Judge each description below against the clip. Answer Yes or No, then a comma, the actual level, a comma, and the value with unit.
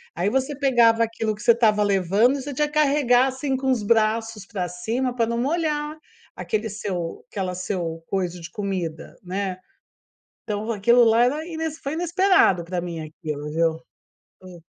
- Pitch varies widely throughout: Yes, wide, 6.3 semitones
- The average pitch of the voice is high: Yes, high, 220 Hz